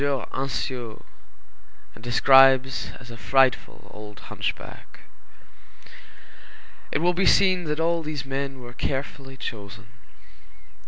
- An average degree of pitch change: Yes, average, 3.1 semitones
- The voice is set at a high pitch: No, low, 135 Hz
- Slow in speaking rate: Yes, slow, 105 wpm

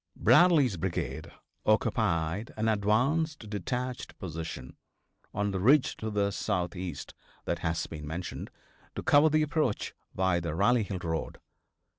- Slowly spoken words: Yes, slow, 130 wpm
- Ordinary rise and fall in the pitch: No, wide, 6.2 semitones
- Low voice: Yes, low, 105 Hz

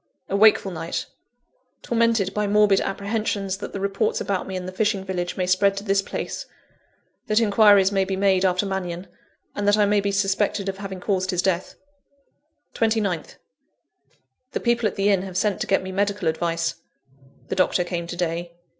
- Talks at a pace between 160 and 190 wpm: Yes, average, 180 wpm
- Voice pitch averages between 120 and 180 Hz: No, high, 195 Hz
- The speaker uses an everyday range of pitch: No, narrow, 1.8 semitones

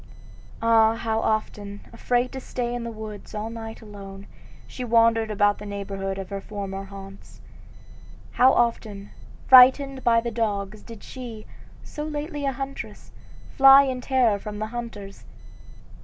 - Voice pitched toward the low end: No, high, 225 Hz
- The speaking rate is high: No, average, 145 wpm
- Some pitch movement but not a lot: Yes, average, 3.3 semitones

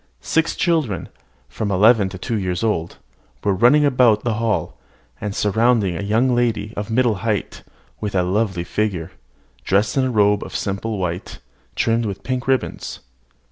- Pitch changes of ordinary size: Yes, average, 3.4 semitones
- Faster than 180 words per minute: No, average, 155 wpm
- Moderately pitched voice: No, low, 105 Hz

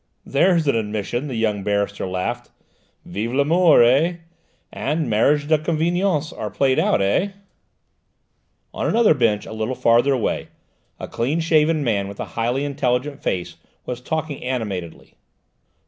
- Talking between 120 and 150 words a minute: Yes, average, 140 wpm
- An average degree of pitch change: No, wide, 5.9 semitones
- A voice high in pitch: No, low, 130 Hz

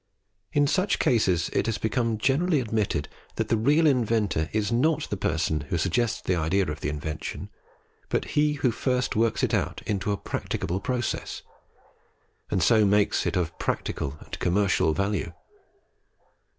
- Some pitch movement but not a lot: No, wide, 5.7 semitones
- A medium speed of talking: Yes, average, 155 wpm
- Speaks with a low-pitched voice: Yes, low, 105 Hz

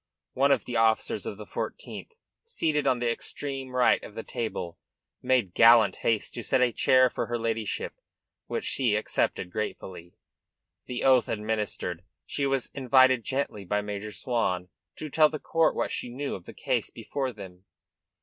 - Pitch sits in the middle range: No, low, 120 Hz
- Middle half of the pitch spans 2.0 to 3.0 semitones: No, average, 4.0 semitones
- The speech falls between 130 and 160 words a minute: No, average, 170 wpm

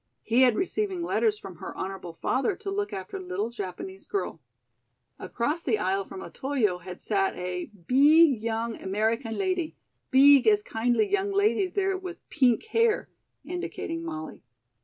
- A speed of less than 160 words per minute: Yes, average, 150 wpm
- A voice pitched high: Yes, very high, 260 Hz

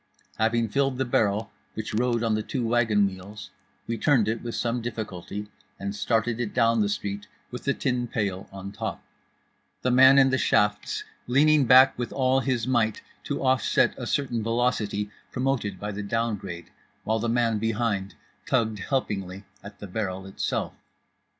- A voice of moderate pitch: No, low, 115 Hz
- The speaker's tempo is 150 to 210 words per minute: Yes, average, 170 wpm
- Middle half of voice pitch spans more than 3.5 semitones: No, average, 3.2 semitones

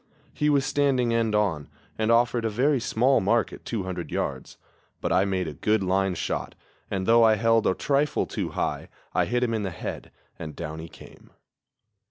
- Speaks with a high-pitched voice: No, low, 110 Hz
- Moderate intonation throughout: Yes, average, 4.4 semitones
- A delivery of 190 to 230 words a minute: Yes, average, 195 wpm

